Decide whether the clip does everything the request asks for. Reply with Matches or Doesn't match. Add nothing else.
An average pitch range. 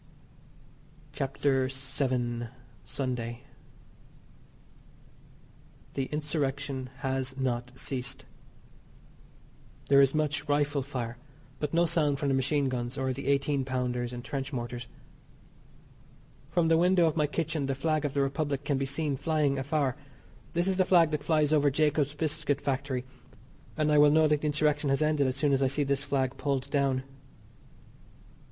Doesn't match